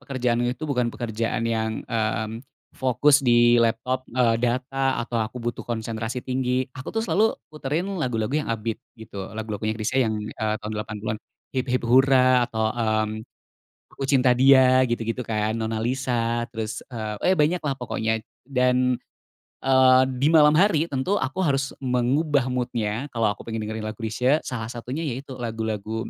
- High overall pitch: No, low, 120 Hz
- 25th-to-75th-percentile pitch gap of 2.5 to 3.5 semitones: Yes, average, 2.9 semitones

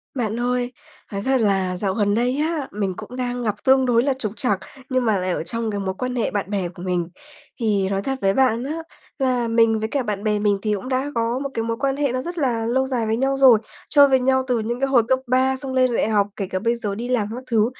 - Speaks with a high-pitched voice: Yes, high, 235 Hz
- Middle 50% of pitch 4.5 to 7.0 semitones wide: No, average, 3.9 semitones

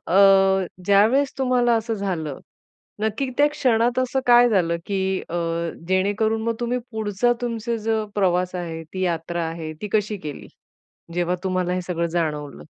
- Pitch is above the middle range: Yes, high, 200 Hz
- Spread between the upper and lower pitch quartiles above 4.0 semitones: Yes, average, 4.6 semitones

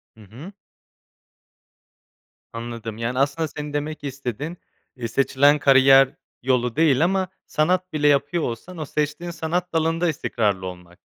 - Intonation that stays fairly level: No, average, 4.7 semitones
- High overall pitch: No, medium, 145 Hz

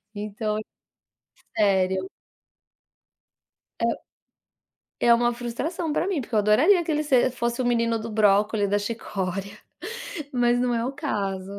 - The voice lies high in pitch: Yes, high, 230 Hz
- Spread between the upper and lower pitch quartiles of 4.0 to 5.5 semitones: No, average, 3.3 semitones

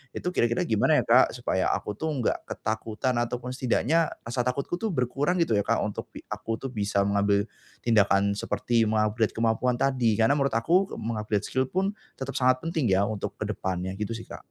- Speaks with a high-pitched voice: No, low, 115 Hz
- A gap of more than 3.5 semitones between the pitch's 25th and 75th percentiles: Yes, average, 4.1 semitones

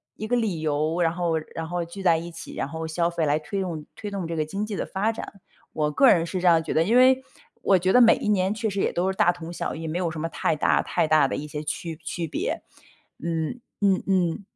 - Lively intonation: No, average, 3.4 semitones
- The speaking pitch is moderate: Yes, medium, 170 Hz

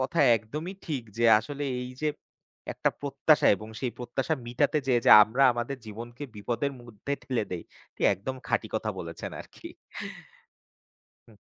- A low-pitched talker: Yes, low, 125 Hz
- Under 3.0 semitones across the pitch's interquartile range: No, average, 3.4 semitones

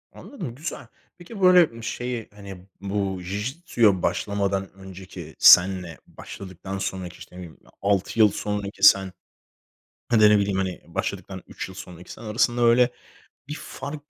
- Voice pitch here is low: Yes, low, 100 Hz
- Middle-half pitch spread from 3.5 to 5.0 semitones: Yes, average, 4.0 semitones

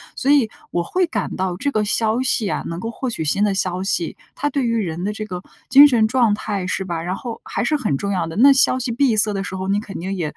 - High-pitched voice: Yes, high, 210 Hz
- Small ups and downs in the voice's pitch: No, average, 4.5 semitones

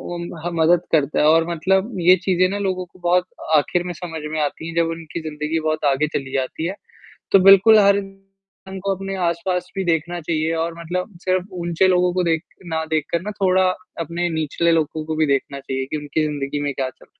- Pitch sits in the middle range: Yes, medium, 170 Hz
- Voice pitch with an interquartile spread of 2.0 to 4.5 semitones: Yes, average, 3.0 semitones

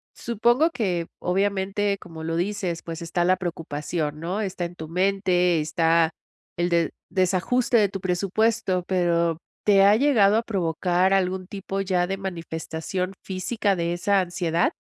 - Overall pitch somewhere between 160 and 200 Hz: Yes, medium, 185 Hz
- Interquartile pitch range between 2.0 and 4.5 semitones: Yes, average, 2.7 semitones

